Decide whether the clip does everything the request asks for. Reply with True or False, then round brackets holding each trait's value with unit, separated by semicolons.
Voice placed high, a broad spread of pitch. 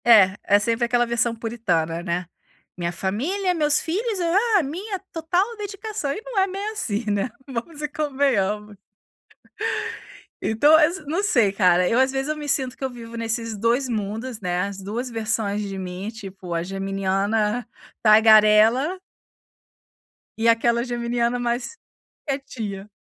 True (235 Hz; 5.7 semitones)